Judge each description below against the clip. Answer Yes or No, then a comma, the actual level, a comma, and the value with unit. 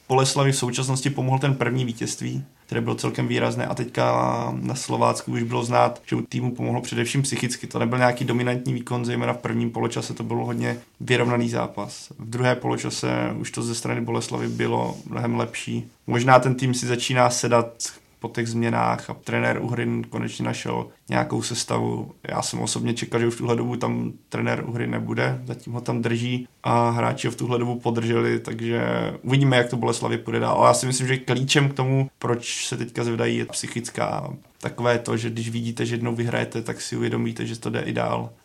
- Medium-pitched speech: No, low, 115 Hz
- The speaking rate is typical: No, fast, 195 wpm